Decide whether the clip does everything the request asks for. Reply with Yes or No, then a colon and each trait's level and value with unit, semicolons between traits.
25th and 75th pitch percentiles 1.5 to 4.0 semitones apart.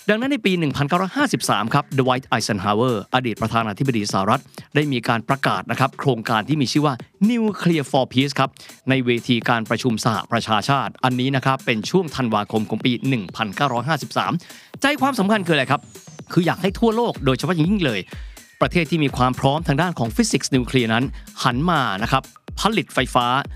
No: average, 5.2 semitones